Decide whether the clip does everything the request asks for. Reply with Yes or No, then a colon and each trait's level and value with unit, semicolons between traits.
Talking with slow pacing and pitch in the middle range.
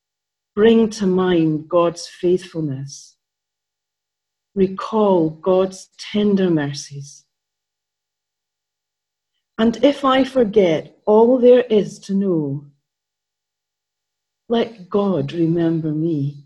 Yes: slow, 80 wpm; medium, 155 Hz